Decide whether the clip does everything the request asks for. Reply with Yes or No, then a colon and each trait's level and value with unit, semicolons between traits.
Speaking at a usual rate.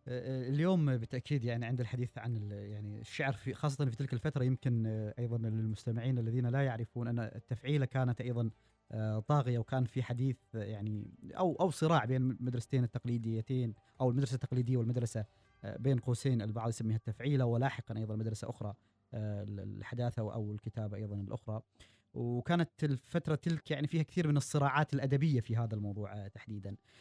No: fast, 145 wpm